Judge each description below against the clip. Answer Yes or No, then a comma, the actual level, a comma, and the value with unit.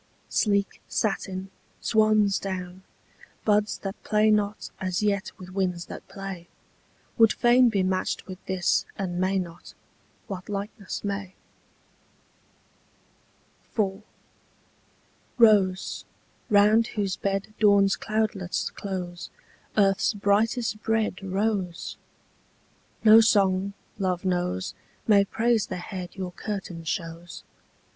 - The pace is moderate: No, slow, 105 wpm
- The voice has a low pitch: No, high, 195 Hz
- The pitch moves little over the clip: Yes, narrow, 2.2 semitones